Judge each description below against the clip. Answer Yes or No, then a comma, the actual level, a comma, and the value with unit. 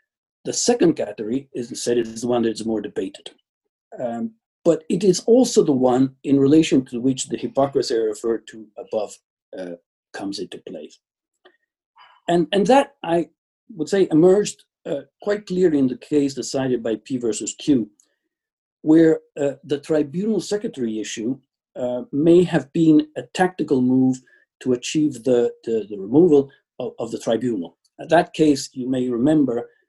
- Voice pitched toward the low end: No, medium, 150 Hz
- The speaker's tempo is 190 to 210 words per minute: No, average, 160 wpm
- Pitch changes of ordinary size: No, wide, 8.4 semitones